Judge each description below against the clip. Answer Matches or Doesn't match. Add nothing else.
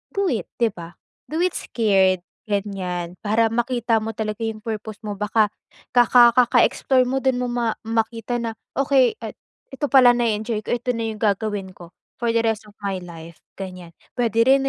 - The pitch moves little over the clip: Doesn't match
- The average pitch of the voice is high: Matches